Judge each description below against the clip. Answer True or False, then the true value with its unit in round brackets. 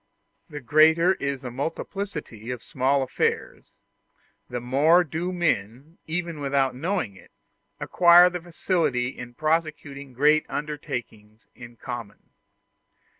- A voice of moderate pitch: True (145 Hz)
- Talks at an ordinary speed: False (110 wpm)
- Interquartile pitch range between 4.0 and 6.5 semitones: True (5.0 semitones)